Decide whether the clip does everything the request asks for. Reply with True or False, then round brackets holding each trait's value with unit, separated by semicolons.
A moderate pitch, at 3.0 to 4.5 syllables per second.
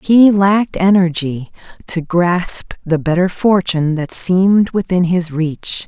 True (180 Hz; 4.0 syllables/s)